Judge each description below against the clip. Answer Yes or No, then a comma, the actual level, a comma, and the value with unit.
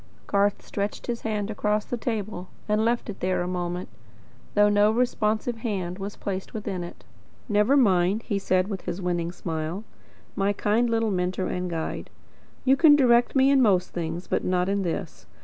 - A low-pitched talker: No, high, 205 Hz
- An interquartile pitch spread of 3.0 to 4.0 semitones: Yes, average, 3.6 semitones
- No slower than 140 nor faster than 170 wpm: No, average, 180 wpm